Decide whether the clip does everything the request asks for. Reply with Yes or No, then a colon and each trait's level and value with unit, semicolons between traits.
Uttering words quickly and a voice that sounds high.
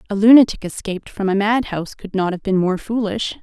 Yes: fast, 210 wpm; high, 205 Hz